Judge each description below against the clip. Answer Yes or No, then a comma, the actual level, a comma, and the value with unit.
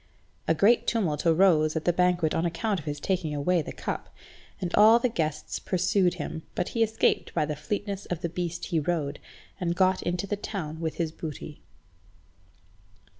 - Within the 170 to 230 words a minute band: Yes, average, 180 wpm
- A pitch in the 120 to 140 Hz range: No, medium, 175 Hz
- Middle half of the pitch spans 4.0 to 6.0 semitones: No, average, 3.4 semitones